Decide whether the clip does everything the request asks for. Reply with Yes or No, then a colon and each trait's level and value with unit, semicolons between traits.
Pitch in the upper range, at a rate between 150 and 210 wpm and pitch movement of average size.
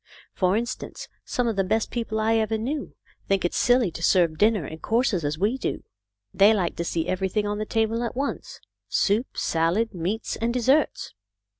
Yes: high, 215 Hz; average, 195 wpm; average, 4.0 semitones